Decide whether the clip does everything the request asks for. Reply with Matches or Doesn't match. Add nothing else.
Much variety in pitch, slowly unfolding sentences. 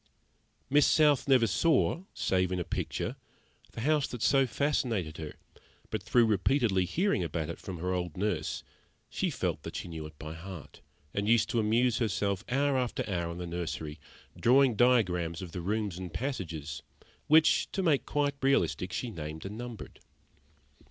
Doesn't match